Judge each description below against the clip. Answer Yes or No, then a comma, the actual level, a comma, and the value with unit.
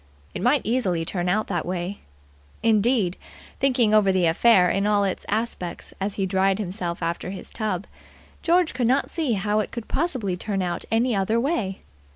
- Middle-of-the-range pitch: No, high, 205 Hz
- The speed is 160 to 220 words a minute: Yes, average, 180 wpm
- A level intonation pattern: No, average, 4.1 semitones